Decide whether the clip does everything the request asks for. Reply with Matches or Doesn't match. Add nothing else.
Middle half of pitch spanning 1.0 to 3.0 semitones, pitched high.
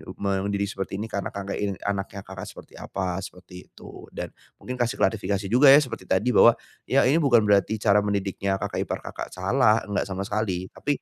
Doesn't match